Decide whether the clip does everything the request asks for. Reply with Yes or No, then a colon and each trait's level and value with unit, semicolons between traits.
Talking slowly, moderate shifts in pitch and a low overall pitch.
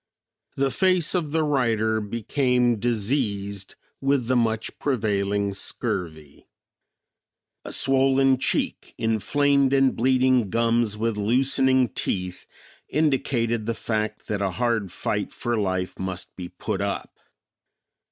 Yes: slow, 115 wpm; average, 4.5 semitones; low, 115 Hz